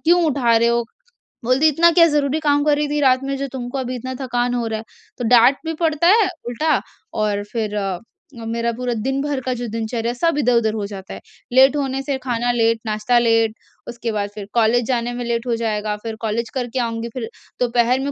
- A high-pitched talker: Yes, high, 245 Hz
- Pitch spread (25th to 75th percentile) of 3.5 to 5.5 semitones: No, average, 3.0 semitones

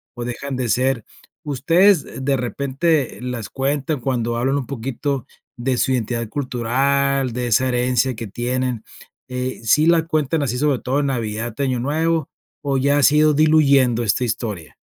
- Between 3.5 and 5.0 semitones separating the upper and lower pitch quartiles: No, average, 2.8 semitones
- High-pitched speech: No, low, 130 Hz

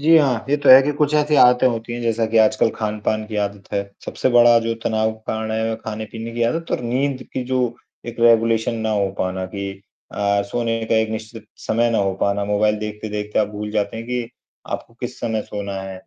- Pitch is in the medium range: No, low, 110 Hz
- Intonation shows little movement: Yes, narrow, 2.0 semitones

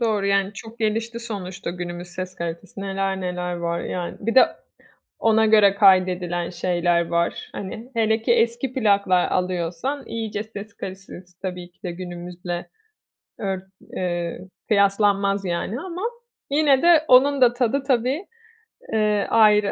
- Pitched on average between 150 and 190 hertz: No, high, 200 Hz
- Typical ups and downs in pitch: Yes, average, 4.1 semitones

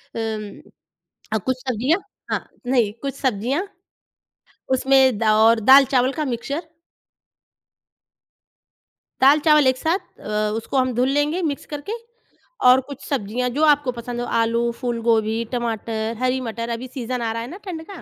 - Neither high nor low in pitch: No, very high, 250 Hz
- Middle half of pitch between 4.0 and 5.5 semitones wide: No, average, 3.3 semitones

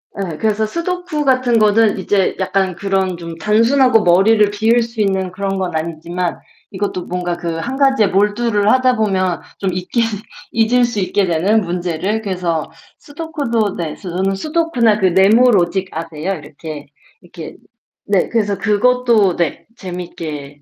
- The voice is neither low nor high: No, high, 195 Hz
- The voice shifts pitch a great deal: No, average, 4.3 semitones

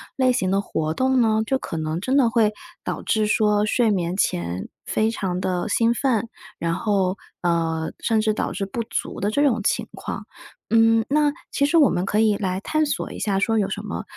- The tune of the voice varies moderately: Yes, average, 3.8 semitones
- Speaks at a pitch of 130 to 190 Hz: No, high, 215 Hz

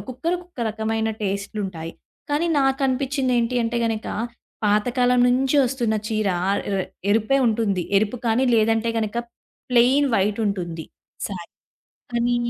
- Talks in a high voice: Yes, high, 225 Hz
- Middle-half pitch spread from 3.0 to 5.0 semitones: Yes, average, 3.3 semitones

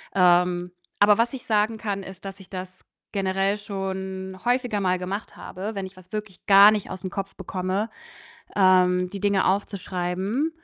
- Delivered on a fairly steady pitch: Yes, narrow, 1.8 semitones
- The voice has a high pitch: Yes, high, 195 Hz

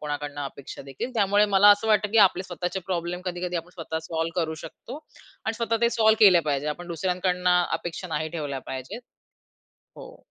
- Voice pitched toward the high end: No, medium, 180 Hz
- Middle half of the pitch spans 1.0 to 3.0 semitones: No, average, 4.1 semitones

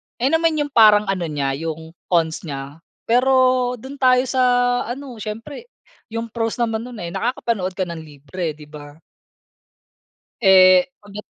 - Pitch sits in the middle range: No, high, 210 Hz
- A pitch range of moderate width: No, wide, 7.3 semitones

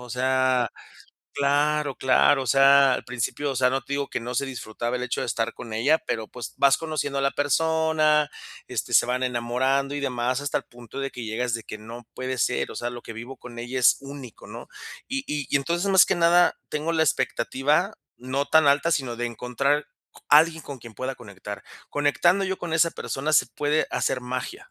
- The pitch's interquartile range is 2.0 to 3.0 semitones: No, average, 3.4 semitones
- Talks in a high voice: No, low, 135 Hz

